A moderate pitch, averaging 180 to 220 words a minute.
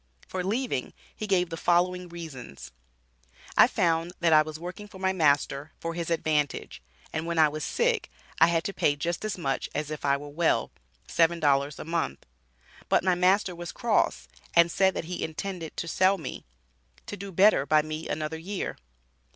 Yes: medium, 165 Hz; average, 185 wpm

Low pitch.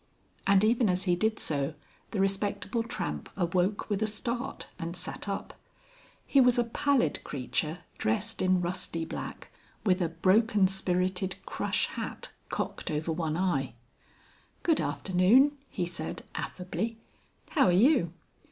No: medium, 185 Hz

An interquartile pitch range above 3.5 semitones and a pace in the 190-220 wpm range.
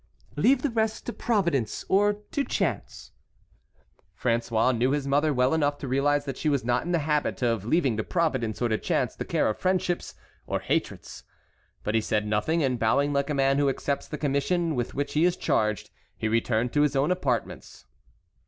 Yes: average, 5.1 semitones; average, 195 wpm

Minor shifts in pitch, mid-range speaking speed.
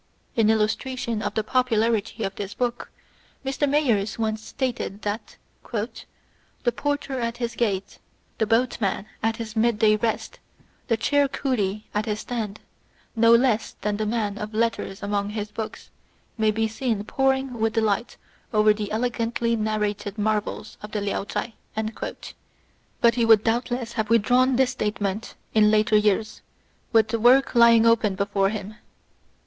Yes: narrow, 2.1 semitones; average, 155 wpm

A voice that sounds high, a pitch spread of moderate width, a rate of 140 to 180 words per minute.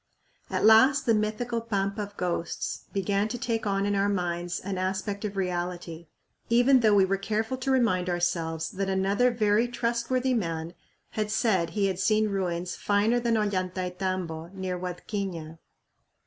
Yes: high, 200 Hz; average, 3.5 semitones; average, 155 wpm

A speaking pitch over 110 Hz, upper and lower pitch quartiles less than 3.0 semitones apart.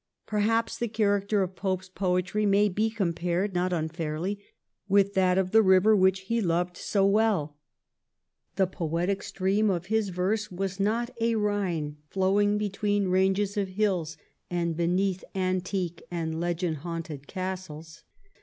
Yes: high, 190 Hz; narrow, 2.6 semitones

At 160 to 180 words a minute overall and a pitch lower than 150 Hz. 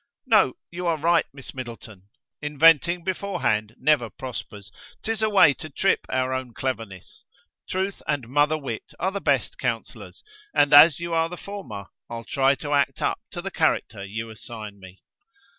Yes: average, 170 wpm; medium, 140 Hz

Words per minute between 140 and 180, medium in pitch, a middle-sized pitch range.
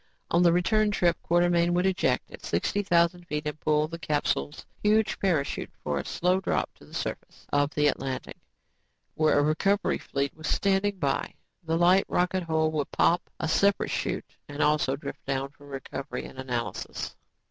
Yes: average, 175 wpm; medium, 160 Hz; average, 3.8 semitones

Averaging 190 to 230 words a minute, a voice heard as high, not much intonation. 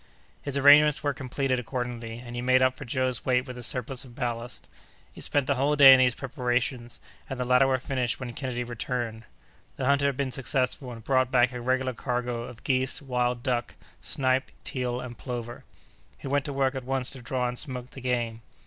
No: fast, 205 wpm; low, 125 Hz; narrow, 1.5 semitones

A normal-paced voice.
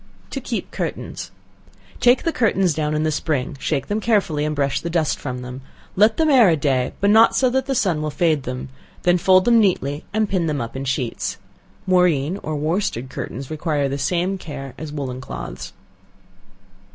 Yes: average, 190 wpm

